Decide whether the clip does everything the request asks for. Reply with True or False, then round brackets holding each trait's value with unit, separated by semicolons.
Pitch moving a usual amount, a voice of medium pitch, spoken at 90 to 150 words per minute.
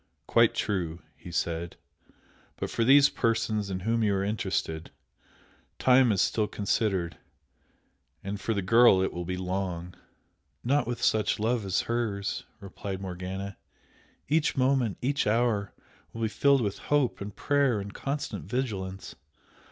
False (4.2 semitones; 105 Hz; 145 wpm)